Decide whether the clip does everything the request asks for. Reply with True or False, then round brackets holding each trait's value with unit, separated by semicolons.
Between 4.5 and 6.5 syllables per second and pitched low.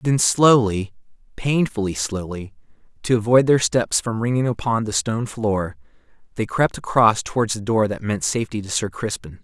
True (5.0 syllables/s; 110 Hz)